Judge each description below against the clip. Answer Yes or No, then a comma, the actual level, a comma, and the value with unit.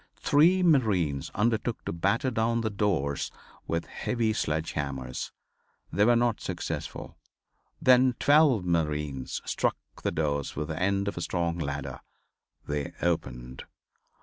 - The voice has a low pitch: Yes, very low, 85 Hz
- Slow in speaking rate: Yes, slow, 130 wpm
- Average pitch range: No, wide, 7.8 semitones